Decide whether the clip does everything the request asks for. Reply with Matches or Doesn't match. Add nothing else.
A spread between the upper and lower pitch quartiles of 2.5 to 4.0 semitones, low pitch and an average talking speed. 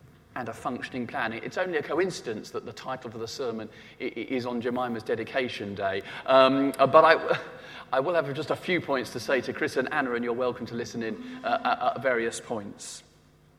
Matches